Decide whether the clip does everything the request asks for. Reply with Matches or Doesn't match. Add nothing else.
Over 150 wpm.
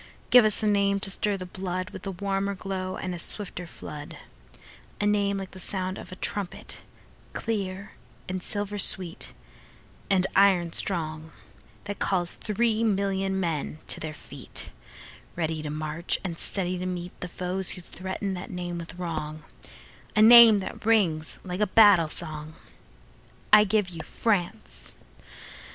Doesn't match